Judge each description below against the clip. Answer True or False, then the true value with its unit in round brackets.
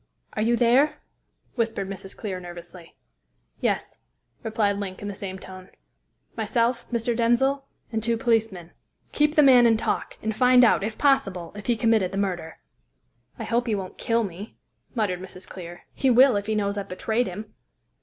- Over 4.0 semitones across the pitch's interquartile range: False (3.7 semitones)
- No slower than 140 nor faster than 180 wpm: True (175 wpm)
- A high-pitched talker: True (220 Hz)